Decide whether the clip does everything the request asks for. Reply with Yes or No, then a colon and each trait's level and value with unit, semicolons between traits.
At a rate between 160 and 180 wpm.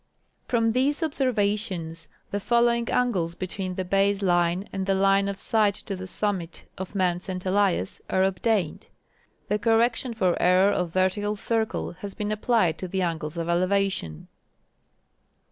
No: average, 150 wpm